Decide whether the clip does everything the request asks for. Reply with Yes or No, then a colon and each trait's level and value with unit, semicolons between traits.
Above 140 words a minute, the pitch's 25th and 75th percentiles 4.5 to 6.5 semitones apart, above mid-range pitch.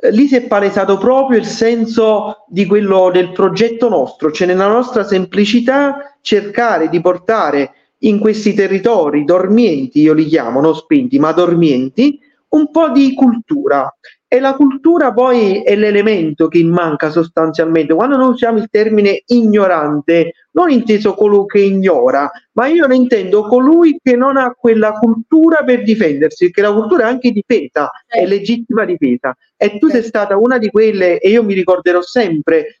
Yes: average, 160 wpm; wide, 5.4 semitones; high, 215 Hz